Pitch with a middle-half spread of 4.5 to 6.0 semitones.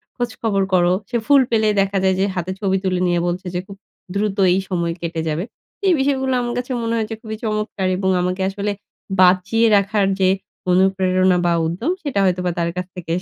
No: average, 3.3 semitones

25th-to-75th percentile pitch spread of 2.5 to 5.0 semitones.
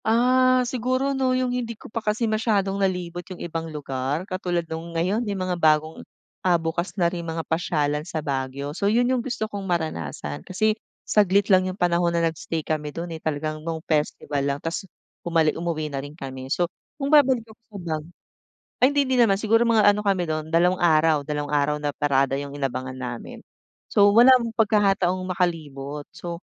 No: wide, 5.4 semitones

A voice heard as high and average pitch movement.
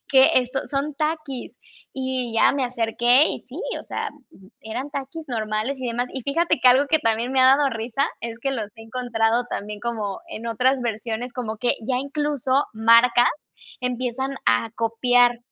Yes: very high, 250 Hz; average, 3.0 semitones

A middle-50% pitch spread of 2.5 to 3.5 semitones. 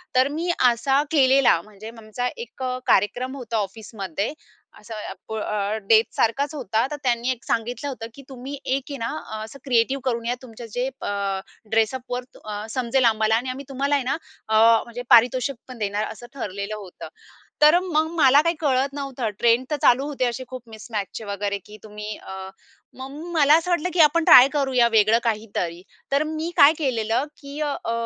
No: average, 4.0 semitones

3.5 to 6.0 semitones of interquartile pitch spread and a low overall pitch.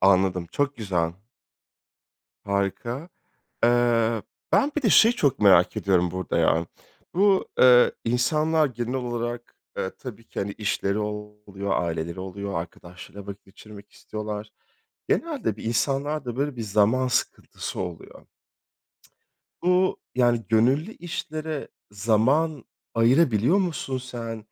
Yes: wide, 5.4 semitones; low, 115 Hz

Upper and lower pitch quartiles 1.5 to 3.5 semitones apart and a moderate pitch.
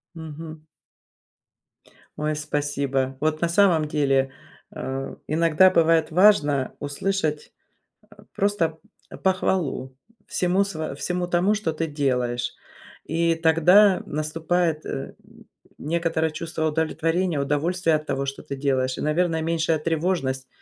Yes: average, 2.9 semitones; medium, 160 Hz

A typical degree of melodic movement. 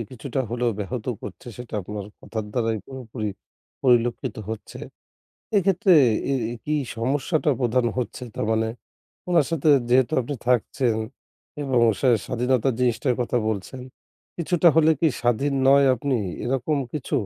Yes: average, 3.3 semitones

